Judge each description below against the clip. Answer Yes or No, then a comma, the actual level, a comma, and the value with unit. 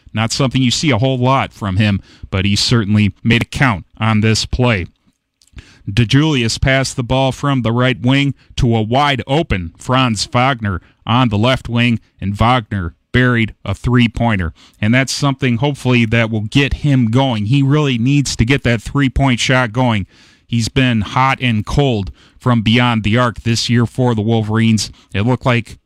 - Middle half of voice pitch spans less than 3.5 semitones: Yes, average, 3.1 semitones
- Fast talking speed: No, average, 180 wpm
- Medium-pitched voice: No, low, 120 Hz